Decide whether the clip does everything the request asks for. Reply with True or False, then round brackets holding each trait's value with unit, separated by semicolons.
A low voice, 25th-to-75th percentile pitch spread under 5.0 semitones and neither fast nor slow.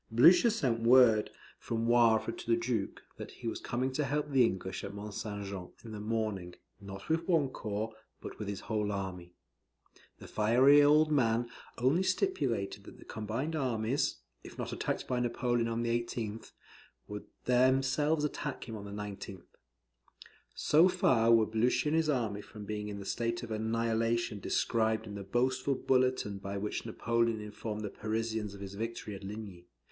True (115 Hz; 3.5 semitones; 175 wpm)